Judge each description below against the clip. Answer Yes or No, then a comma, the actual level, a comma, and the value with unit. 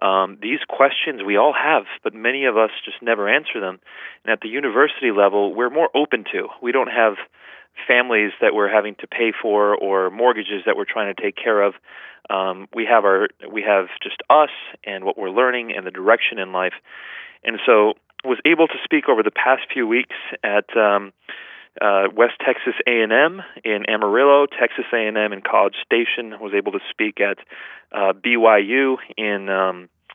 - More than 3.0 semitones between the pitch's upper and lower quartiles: Yes, average, 3.9 semitones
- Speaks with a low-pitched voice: Yes, low, 105 Hz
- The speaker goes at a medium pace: Yes, average, 185 wpm